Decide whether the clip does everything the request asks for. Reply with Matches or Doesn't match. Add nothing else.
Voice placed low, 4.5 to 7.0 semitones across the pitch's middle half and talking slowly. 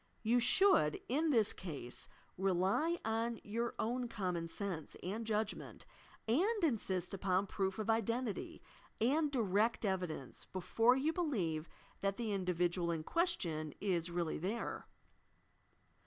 Doesn't match